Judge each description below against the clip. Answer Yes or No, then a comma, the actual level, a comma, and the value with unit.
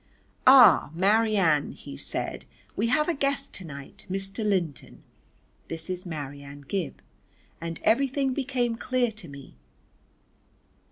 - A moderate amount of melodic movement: No, wide, 7.5 semitones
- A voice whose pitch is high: Yes, high, 195 Hz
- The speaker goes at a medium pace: No, slow, 120 wpm